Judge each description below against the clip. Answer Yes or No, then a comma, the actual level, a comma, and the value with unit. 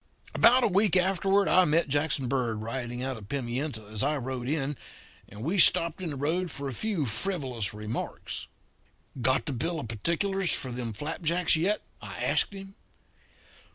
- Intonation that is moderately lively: No, wide, 6.6 semitones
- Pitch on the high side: No, medium, 145 Hz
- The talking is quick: No, average, 170 wpm